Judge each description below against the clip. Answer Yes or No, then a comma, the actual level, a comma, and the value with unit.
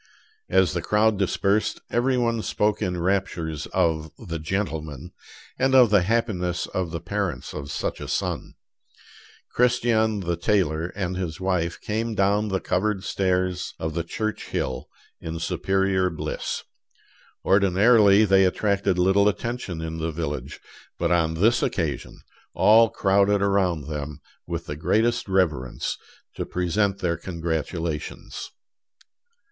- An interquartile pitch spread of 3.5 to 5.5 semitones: Yes, average, 4.0 semitones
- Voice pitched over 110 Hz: No, very low, 95 Hz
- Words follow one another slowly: Yes, slow, 130 wpm